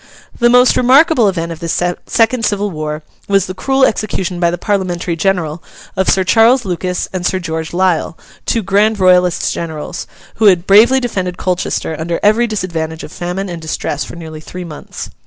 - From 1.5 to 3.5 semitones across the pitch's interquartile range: No, average, 4.0 semitones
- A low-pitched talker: No, medium, 185 Hz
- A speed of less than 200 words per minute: Yes, average, 175 wpm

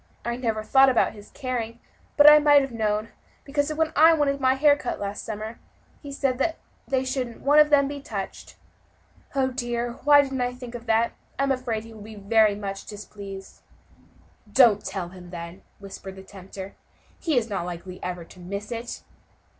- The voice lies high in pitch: Yes, high, 235 Hz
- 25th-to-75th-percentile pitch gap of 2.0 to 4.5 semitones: No, average, 5.1 semitones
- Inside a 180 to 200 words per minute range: Yes, average, 185 wpm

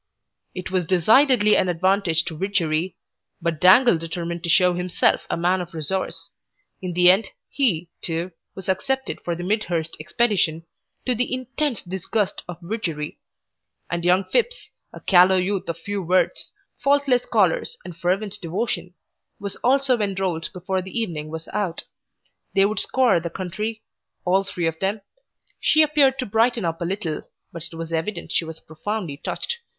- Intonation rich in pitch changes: No, average, 4.3 semitones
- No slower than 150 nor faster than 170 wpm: Yes, average, 160 wpm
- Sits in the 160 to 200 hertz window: Yes, medium, 185 Hz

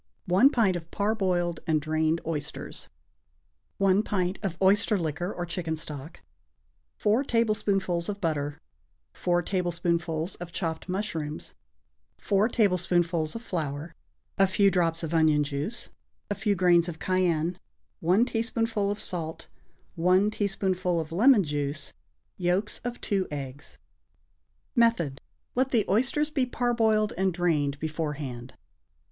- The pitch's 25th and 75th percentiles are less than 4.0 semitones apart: No, average, 4.3 semitones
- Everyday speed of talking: No, slow, 125 wpm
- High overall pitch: No, medium, 180 Hz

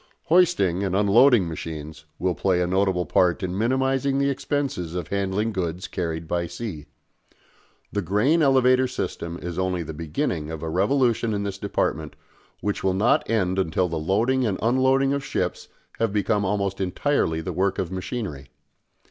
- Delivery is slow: No, average, 165 wpm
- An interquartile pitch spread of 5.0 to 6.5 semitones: Yes, wide, 5.4 semitones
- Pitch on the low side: Yes, very low, 95 Hz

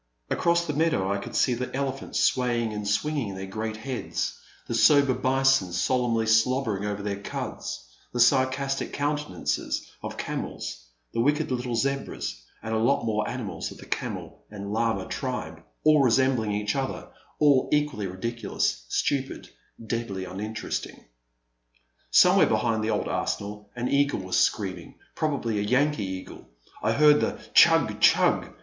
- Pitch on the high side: No, low, 115 Hz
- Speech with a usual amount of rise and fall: Yes, average, 4.8 semitones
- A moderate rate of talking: Yes, average, 145 wpm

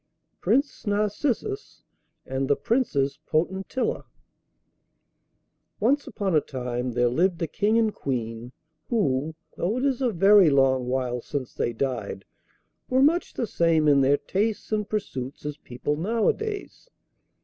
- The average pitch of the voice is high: No, medium, 165 Hz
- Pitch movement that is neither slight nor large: No, wide, 8.8 semitones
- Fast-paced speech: No, slow, 135 wpm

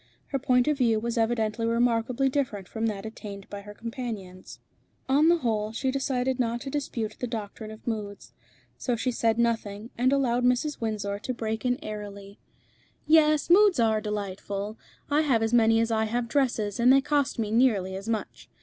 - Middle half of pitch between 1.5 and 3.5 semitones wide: Yes, average, 3.0 semitones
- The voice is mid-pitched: No, high, 230 Hz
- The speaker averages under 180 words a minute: No, average, 185 wpm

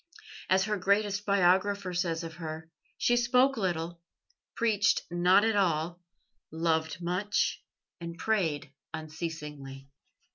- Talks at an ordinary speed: No, slow, 110 wpm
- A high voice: No, medium, 175 Hz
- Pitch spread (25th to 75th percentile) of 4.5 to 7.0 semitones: No, average, 4.0 semitones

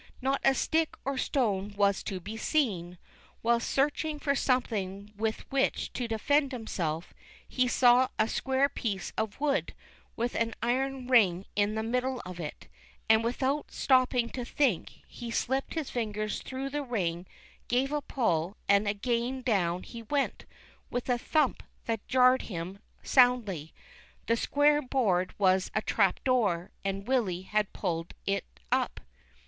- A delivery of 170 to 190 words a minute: No, average, 150 wpm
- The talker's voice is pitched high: Yes, high, 235 Hz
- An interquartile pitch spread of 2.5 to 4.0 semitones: No, average, 4.8 semitones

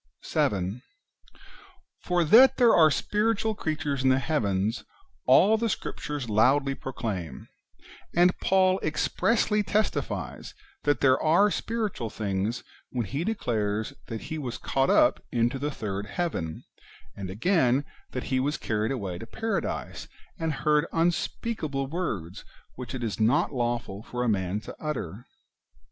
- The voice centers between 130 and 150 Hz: Yes, low, 135 Hz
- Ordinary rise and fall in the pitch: No, wide, 7.5 semitones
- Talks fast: No, slow, 135 wpm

